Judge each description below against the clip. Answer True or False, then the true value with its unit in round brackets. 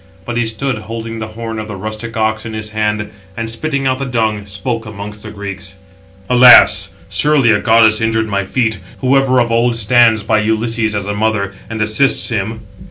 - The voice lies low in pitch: True (110 Hz)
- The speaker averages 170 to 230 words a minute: True (195 wpm)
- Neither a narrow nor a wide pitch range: False (1.8 semitones)